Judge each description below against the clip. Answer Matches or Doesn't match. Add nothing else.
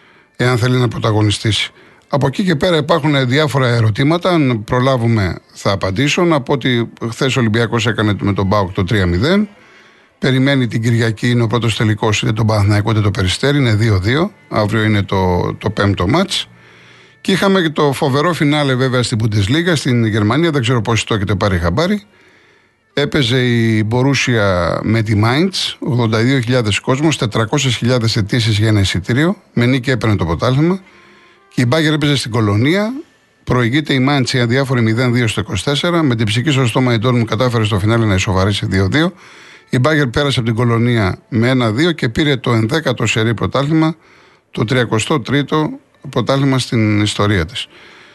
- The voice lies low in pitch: Matches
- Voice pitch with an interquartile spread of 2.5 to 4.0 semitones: Doesn't match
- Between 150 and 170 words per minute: Matches